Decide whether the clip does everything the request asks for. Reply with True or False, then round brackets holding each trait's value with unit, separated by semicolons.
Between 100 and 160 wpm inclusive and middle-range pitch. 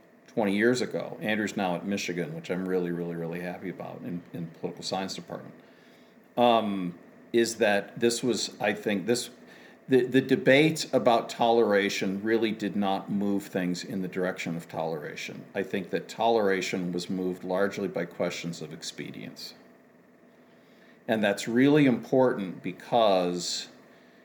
False (145 wpm; 100 Hz)